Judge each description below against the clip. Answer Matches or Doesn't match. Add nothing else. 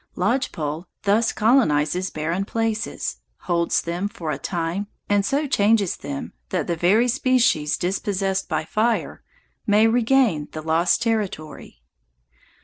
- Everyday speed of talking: Doesn't match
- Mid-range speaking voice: Doesn't match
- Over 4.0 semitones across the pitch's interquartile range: Matches